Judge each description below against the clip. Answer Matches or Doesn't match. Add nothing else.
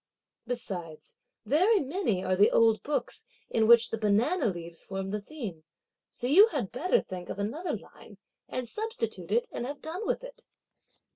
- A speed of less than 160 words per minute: Doesn't match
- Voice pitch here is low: Doesn't match